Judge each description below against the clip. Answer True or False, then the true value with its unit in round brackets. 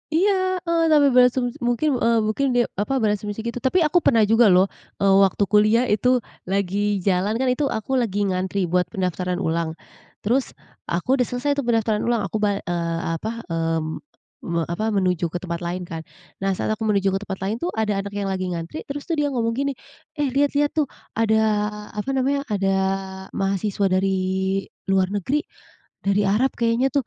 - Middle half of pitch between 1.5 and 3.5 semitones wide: False (5.0 semitones)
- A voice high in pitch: True (210 Hz)